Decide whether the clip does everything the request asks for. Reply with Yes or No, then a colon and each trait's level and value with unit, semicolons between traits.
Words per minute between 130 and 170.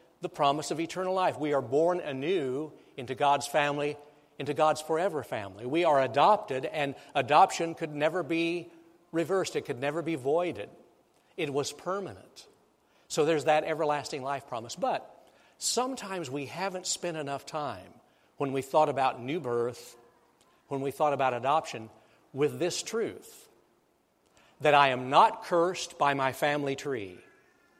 Yes: average, 150 wpm